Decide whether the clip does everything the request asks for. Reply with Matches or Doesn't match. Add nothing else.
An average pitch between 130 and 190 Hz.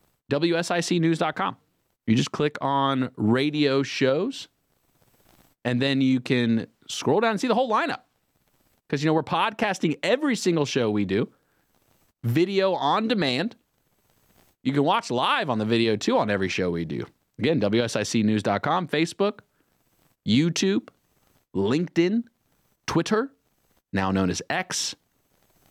Matches